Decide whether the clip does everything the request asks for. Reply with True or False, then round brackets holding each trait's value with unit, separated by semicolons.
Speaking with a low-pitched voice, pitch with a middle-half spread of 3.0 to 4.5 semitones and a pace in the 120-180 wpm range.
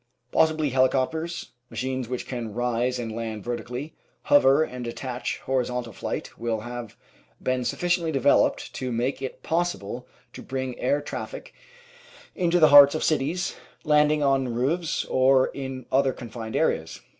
True (130 Hz; 3.4 semitones; 145 wpm)